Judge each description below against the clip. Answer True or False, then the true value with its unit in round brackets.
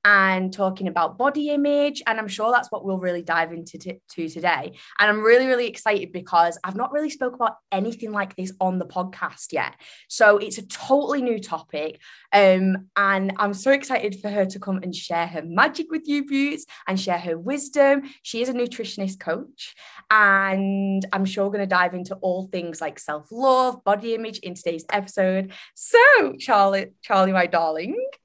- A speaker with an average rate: True (185 wpm)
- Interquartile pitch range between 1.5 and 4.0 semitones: False (4.6 semitones)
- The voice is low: False (200 Hz)